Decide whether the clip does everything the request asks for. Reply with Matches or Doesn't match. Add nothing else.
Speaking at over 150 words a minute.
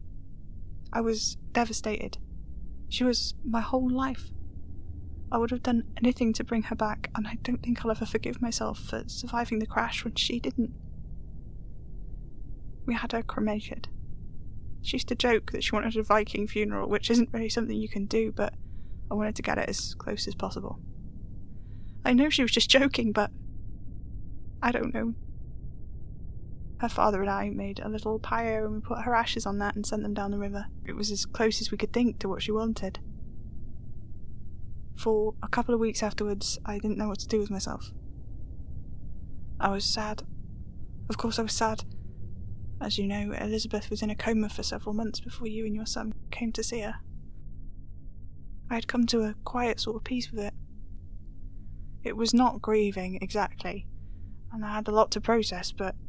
Matches